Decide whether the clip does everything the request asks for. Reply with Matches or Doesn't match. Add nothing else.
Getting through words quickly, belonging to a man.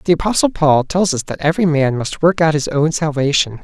Matches